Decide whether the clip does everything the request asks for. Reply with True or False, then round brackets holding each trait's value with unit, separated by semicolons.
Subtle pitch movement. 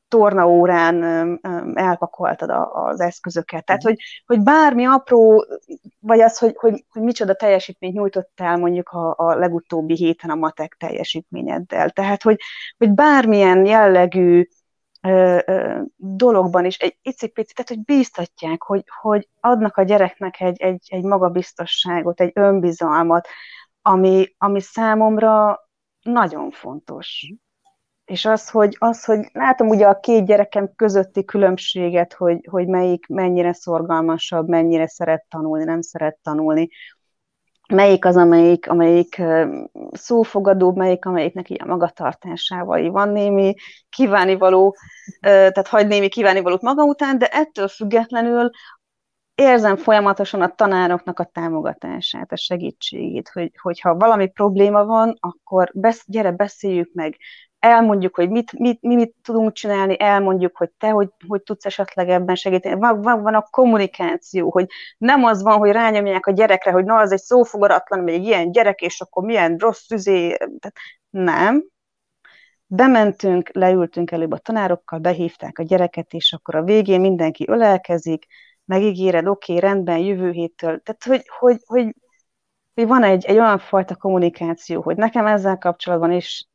False (3.8 semitones)